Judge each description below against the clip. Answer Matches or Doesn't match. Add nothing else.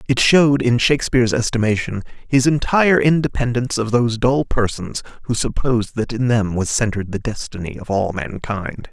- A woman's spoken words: Doesn't match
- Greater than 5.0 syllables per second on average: Matches